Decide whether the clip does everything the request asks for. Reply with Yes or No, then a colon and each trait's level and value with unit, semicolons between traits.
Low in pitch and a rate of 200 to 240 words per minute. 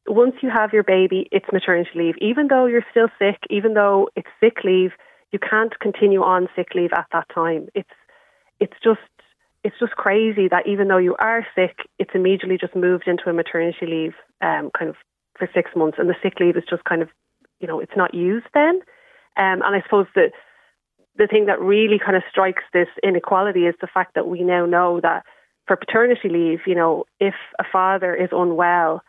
No: high, 190 Hz; fast, 205 wpm